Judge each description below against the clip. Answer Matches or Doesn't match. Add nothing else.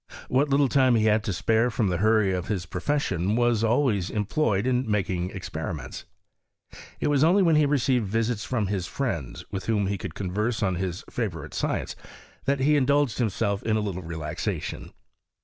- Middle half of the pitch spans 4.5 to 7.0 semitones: Matches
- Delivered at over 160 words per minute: Matches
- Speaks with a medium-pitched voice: Doesn't match